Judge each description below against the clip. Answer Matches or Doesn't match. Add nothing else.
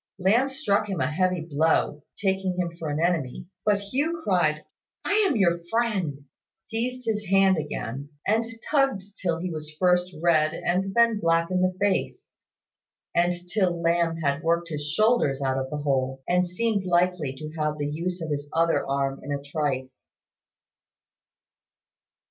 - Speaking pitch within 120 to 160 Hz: Doesn't match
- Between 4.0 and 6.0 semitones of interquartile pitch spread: Matches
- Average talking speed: Matches